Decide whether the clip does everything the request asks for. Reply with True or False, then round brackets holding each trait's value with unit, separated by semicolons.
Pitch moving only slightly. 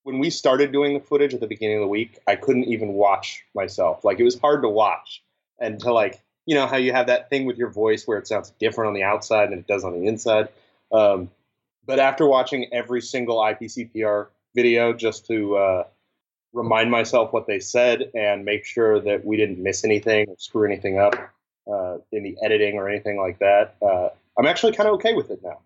False (3.4 semitones)